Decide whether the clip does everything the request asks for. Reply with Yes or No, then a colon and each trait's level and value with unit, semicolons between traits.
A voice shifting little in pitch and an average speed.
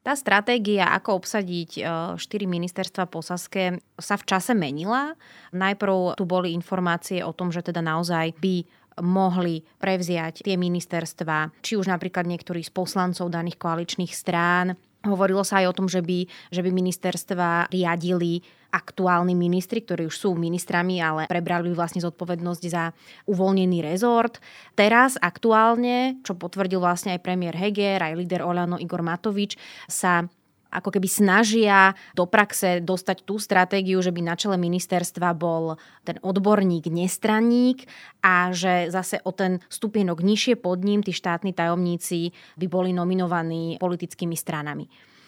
Yes: narrow, 2.0 semitones; average, 140 wpm